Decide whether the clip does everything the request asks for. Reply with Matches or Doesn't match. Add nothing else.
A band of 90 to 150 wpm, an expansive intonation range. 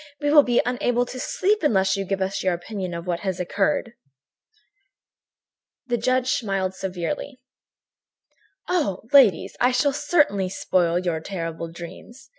Matches